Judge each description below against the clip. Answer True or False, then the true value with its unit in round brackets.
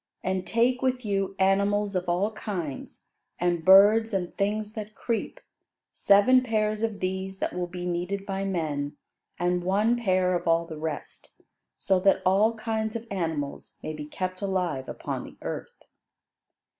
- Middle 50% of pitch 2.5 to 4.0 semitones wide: True (3.2 semitones)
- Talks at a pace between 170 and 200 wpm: False (155 wpm)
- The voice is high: True (195 Hz)